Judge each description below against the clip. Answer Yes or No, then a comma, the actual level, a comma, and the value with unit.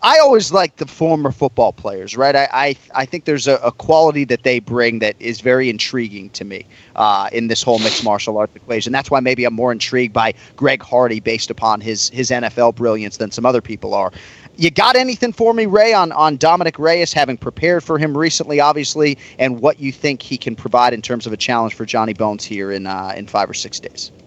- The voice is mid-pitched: No, low, 125 Hz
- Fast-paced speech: Yes, fast, 230 wpm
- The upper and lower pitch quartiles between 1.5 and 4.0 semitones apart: No, average, 5.0 semitones